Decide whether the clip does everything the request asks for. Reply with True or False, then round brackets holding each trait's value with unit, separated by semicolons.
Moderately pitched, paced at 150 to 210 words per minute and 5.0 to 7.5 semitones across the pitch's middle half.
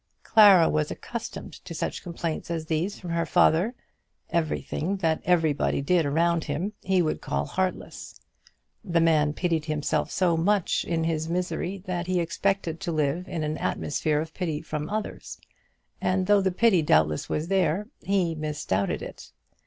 False (170 Hz; 160 wpm; 3.1 semitones)